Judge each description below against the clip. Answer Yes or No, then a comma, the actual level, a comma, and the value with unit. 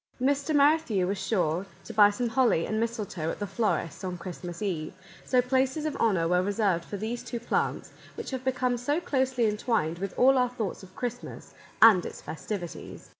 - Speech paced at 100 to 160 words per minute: No, average, 185 wpm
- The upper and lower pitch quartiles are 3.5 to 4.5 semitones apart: No, wide, 5.4 semitones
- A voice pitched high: Yes, high, 220 Hz